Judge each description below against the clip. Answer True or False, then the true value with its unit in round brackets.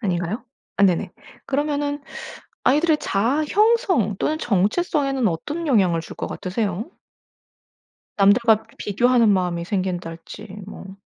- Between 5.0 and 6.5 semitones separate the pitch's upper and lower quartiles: False (7.5 semitones)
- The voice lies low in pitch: False (220 Hz)